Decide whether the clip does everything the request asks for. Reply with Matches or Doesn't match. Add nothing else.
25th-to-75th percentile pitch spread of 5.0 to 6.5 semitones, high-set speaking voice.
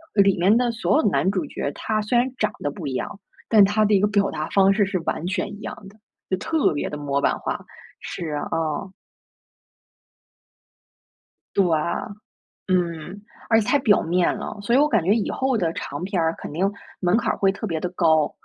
Doesn't match